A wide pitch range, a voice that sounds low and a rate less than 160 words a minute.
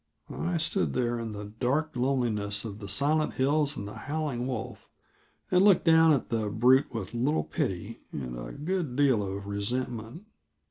No: wide, 6.3 semitones; low, 125 Hz; average, 170 wpm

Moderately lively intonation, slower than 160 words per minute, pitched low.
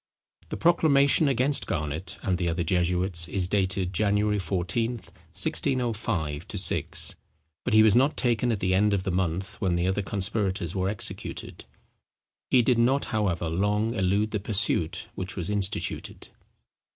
Yes: average, 3.4 semitones; average, 150 wpm; low, 100 Hz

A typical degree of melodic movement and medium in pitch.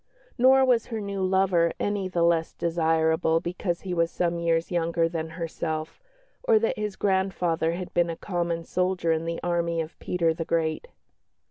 No: narrow, 2.3 semitones; medium, 170 Hz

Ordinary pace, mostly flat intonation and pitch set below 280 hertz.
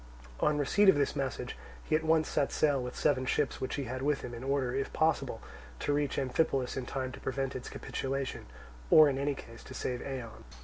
No: fast, 215 wpm; narrow, 2.2 semitones; low, 135 Hz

